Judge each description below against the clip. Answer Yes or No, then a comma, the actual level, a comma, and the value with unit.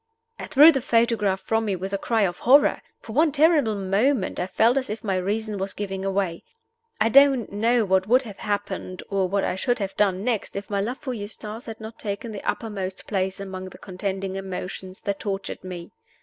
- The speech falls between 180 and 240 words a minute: Yes, fast, 205 wpm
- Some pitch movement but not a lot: Yes, average, 3.1 semitones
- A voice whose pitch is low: No, high, 205 Hz